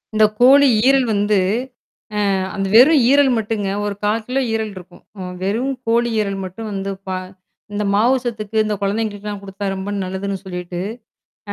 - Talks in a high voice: Yes, high, 210 Hz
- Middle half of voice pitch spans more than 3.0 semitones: No, average, 2.7 semitones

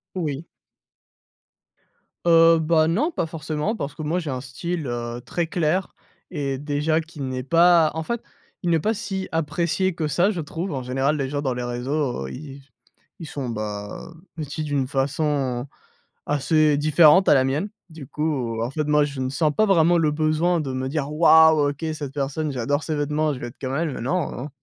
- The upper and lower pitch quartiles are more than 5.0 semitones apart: No, average, 3.4 semitones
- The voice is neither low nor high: Yes, medium, 150 Hz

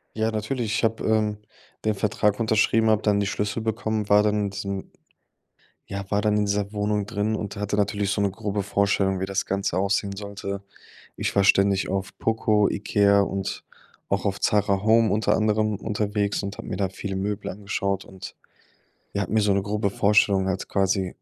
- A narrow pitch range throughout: Yes, narrow, 1.3 semitones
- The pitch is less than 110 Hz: Yes, low, 100 Hz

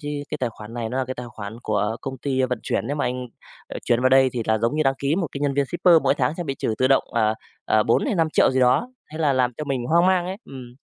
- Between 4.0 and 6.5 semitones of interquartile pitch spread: No, average, 3.5 semitones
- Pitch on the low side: Yes, low, 130 Hz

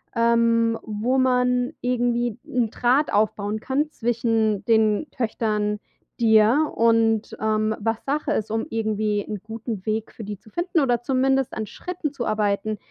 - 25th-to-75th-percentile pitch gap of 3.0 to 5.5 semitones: No, narrow, 2.5 semitones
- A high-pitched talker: Yes, high, 225 Hz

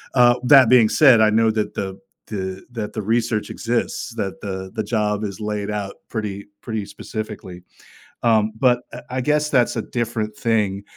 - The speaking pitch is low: Yes, low, 110 Hz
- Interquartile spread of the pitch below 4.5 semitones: Yes, narrow, 2.4 semitones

